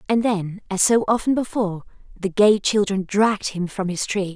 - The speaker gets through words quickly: No, average, 195 wpm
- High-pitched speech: Yes, high, 200 Hz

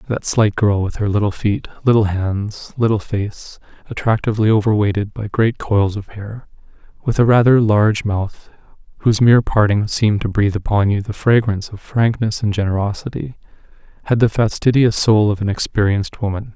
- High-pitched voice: No, low, 105 Hz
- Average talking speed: Yes, average, 165 wpm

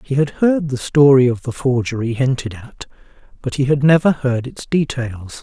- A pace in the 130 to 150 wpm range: No, average, 190 wpm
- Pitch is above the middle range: No, low, 130 Hz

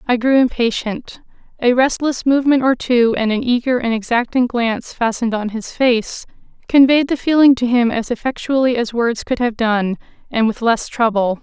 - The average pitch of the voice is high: Yes, high, 240 Hz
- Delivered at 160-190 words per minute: Yes, average, 180 wpm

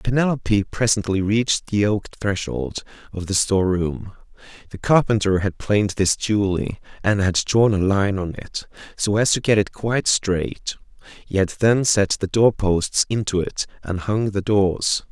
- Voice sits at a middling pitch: No, low, 100 Hz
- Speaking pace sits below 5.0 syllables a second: Yes, 4.4 syllables/s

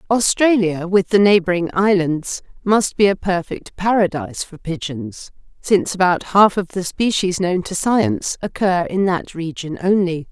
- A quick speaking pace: No, average, 150 wpm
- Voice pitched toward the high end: No, medium, 180 Hz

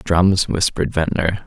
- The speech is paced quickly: No, slow, 125 wpm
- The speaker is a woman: No, male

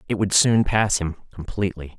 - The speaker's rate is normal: Yes, average, 180 wpm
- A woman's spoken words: No, male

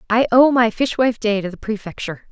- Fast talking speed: Yes, fast, 210 wpm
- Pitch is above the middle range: Yes, high, 225 Hz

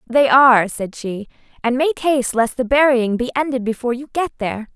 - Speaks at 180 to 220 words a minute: Yes, average, 200 wpm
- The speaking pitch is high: Yes, very high, 250 Hz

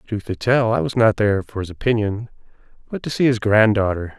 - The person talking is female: No, male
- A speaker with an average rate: No, fast, 215 wpm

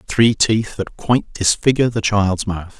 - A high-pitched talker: No, low, 105 Hz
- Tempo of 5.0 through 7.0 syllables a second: No, 4.6 syllables/s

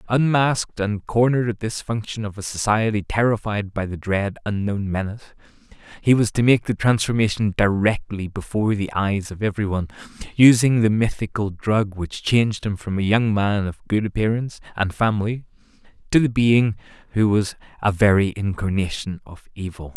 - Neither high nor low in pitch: No, low, 105 Hz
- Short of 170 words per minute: Yes, average, 160 wpm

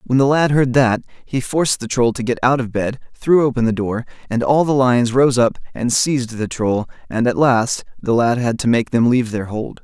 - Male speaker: Yes, male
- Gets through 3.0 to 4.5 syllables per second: No, 5.1 syllables/s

